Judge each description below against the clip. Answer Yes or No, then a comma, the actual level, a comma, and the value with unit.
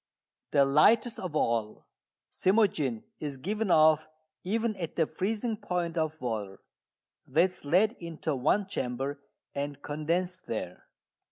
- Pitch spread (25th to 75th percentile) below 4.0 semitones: No, average, 5.1 semitones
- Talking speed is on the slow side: Yes, slow, 125 wpm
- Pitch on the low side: No, medium, 160 Hz